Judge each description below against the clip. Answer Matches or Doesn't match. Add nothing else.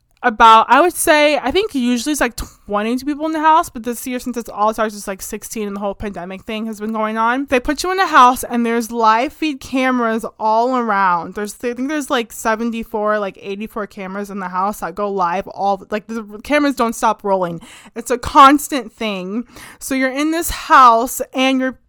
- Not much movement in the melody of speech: Doesn't match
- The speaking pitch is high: Matches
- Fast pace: Matches